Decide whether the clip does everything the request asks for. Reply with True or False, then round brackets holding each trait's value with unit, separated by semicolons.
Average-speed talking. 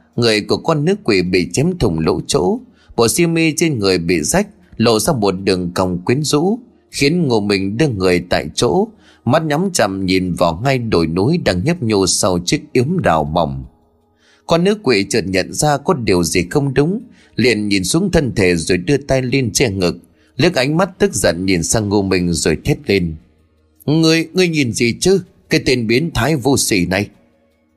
True (200 wpm)